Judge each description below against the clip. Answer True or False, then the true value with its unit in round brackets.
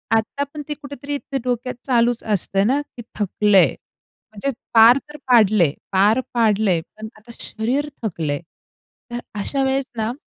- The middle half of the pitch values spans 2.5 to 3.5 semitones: False (4.4 semitones)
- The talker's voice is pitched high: True (230 Hz)